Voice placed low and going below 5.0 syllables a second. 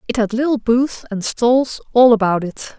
No: high, 230 Hz; 4.5 syllables/s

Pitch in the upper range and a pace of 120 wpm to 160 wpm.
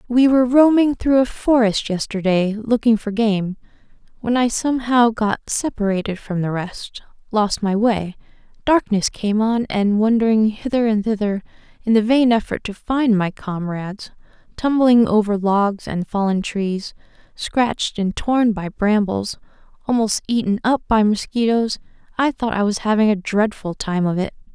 Yes: high, 220 Hz; average, 155 wpm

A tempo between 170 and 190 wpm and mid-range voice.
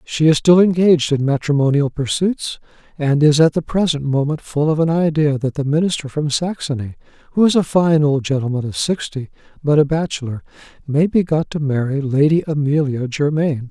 Yes: average, 180 wpm; medium, 150 Hz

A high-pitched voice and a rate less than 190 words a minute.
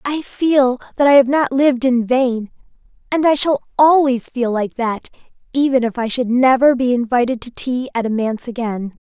No: very high, 250 Hz; average, 195 wpm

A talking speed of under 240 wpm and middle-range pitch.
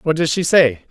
No: fast, 265 wpm; medium, 150 Hz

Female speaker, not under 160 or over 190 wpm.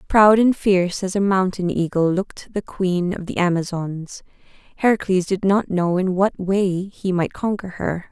Yes: female; average, 180 wpm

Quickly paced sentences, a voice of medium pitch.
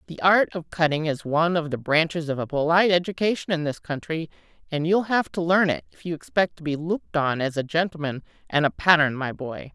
Yes: fast, 230 wpm; medium, 160 Hz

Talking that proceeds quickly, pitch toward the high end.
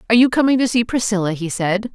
Yes: fast, 245 wpm; high, 220 Hz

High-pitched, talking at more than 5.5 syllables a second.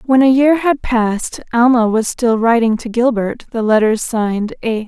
No: high, 235 Hz; 4.7 syllables/s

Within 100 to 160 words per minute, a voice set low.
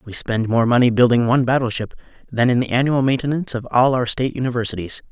No: average, 200 wpm; low, 120 Hz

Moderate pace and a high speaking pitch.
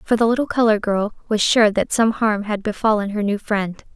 No: fast, 225 wpm; high, 215 Hz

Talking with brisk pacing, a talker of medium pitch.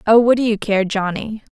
No: fast, 235 wpm; high, 215 Hz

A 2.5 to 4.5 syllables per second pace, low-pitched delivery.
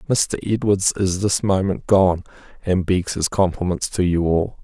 Yes: 4.3 syllables/s; very low, 95 Hz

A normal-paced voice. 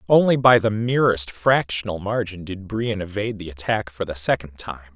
Yes: average, 180 wpm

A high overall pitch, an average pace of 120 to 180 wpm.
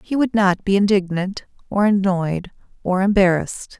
Yes: high, 195 Hz; average, 140 wpm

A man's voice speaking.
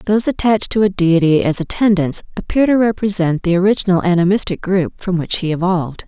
No: female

